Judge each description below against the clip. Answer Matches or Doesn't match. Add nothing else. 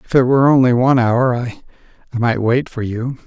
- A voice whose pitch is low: Matches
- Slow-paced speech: Doesn't match